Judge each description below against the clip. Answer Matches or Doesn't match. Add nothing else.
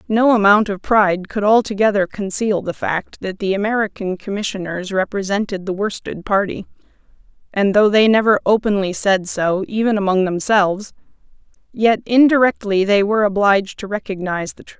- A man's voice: Doesn't match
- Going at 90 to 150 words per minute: Matches